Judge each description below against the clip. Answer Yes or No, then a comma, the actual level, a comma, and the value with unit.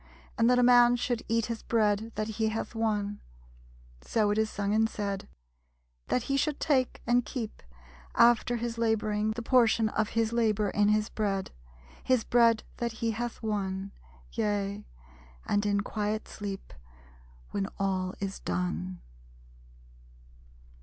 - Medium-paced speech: Yes, average, 145 wpm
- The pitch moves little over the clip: Yes, narrow, 2.3 semitones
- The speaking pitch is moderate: No, high, 220 Hz